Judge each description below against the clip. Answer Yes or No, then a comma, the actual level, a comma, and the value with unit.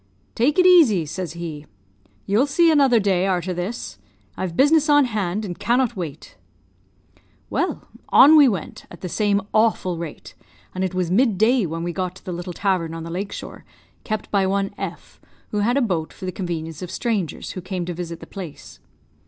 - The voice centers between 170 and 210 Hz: Yes, high, 190 Hz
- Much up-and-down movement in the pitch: No, average, 4.9 semitones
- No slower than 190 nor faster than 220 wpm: Yes, average, 195 wpm